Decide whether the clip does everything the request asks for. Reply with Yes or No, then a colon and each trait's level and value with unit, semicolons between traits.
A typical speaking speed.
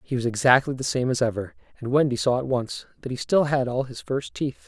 No: fast, 255 wpm